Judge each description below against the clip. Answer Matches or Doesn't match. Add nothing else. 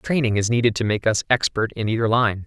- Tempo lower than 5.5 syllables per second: Doesn't match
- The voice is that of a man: Matches